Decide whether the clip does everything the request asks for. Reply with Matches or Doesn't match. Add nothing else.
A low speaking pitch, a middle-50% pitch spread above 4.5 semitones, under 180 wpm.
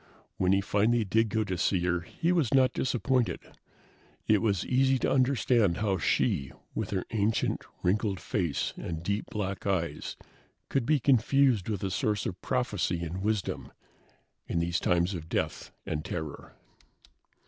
Matches